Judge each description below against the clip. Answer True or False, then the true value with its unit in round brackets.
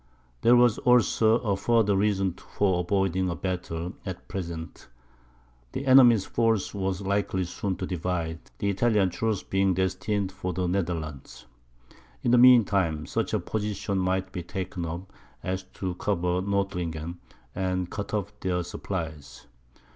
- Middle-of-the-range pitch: False (95 Hz)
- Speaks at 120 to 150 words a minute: True (145 wpm)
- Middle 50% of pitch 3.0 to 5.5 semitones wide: False (2.4 semitones)